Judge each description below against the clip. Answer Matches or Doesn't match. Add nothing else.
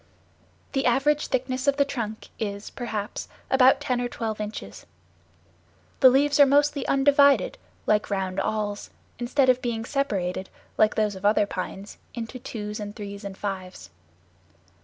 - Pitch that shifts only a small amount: Doesn't match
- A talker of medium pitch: Doesn't match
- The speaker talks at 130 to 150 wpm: Matches